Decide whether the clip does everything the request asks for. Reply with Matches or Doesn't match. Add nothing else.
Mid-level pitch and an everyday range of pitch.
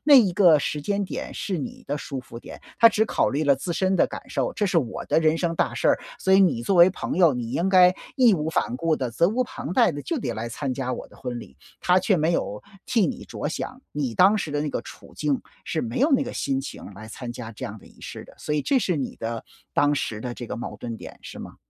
Doesn't match